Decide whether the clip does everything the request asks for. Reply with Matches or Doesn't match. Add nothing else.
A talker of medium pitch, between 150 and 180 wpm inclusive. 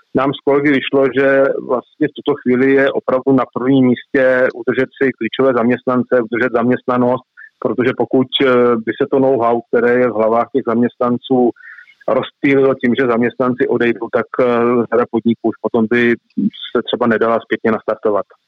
Doesn't match